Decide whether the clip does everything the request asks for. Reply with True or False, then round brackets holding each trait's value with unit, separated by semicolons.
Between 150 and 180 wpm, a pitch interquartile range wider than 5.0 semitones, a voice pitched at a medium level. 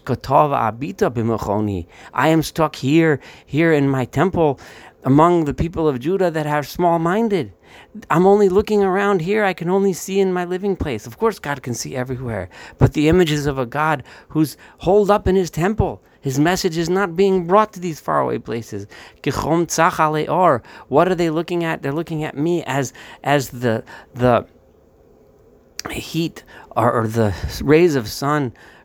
True (160 wpm; 5.5 semitones; 155 Hz)